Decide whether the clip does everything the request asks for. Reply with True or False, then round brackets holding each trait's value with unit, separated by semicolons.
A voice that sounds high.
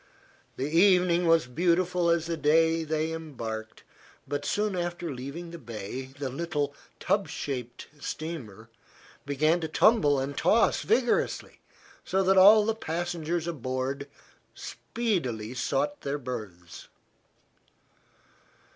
False (160 Hz)